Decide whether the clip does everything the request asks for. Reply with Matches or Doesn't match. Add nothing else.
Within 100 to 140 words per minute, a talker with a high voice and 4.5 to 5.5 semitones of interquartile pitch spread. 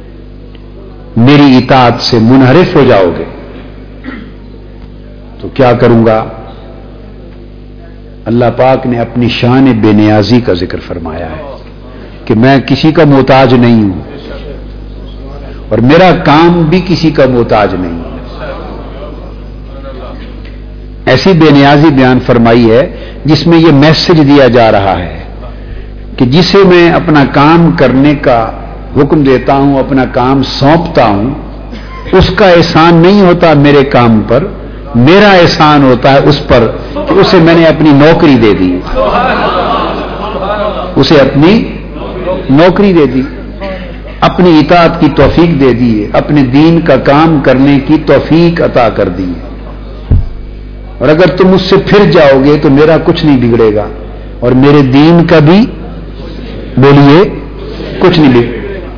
Doesn't match